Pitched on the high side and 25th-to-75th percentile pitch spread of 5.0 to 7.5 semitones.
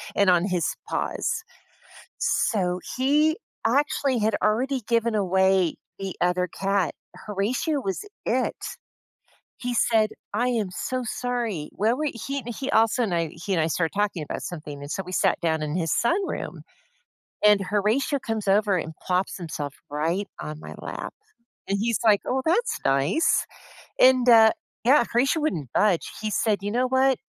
Yes: high, 210 Hz; wide, 5.4 semitones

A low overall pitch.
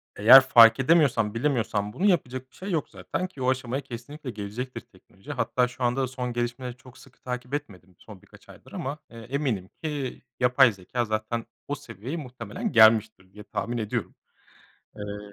Yes: low, 125 Hz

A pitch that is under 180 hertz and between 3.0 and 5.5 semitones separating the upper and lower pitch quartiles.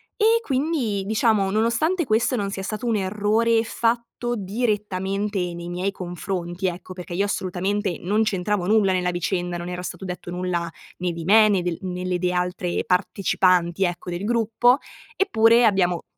No: high, 195 Hz; average, 3.6 semitones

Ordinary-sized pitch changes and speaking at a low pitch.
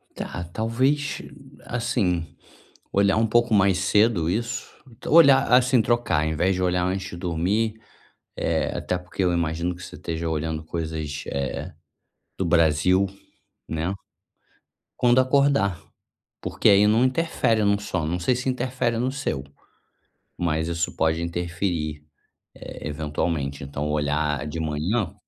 No: wide, 6.2 semitones; very low, 90 Hz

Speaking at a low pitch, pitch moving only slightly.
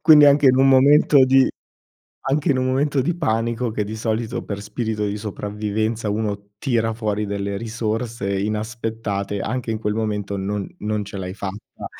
No: low, 110 Hz; average, 3.5 semitones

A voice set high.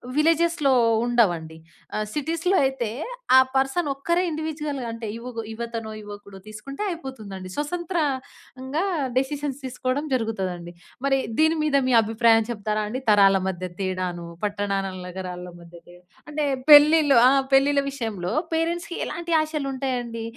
Yes: very high, 255 Hz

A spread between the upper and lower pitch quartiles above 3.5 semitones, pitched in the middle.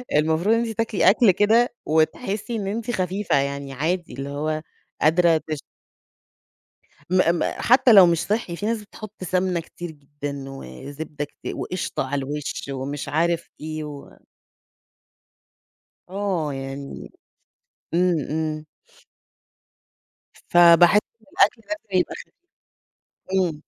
Yes: average, 5.1 semitones; medium, 170 Hz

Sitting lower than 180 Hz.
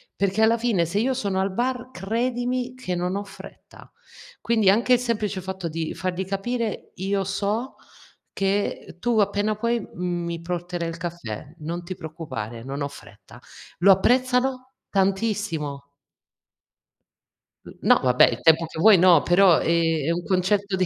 No: high, 190 Hz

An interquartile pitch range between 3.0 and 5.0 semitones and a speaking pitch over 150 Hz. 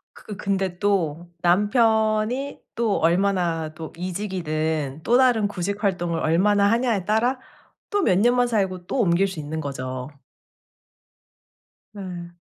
Yes: average, 4.3 semitones; high, 190 Hz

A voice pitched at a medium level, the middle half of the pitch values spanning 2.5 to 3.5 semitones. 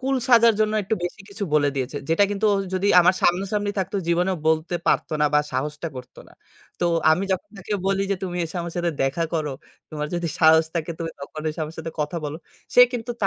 No: medium, 175 Hz; average, 4.2 semitones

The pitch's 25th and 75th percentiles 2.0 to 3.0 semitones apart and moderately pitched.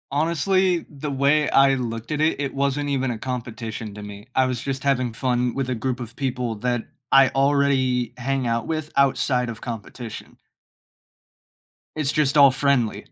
No: narrow, 2.5 semitones; low, 130 Hz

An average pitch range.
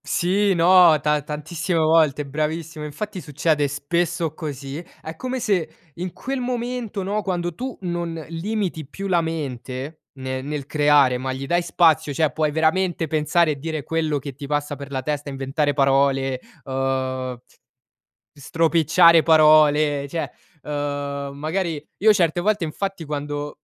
Yes: average, 3.3 semitones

